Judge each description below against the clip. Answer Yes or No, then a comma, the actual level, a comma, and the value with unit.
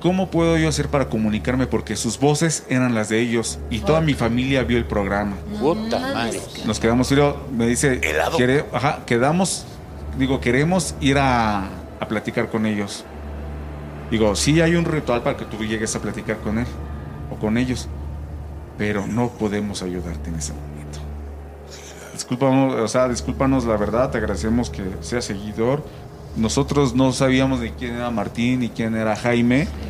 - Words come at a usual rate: Yes, average, 160 wpm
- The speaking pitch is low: Yes, low, 115 Hz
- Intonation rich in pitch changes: Yes, wide, 5.8 semitones